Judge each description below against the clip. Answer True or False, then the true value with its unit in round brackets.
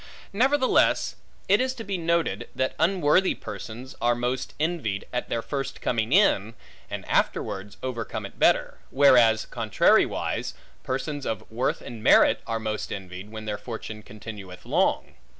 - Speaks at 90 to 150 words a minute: True (145 wpm)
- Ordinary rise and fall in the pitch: False (5.8 semitones)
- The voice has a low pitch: True (120 Hz)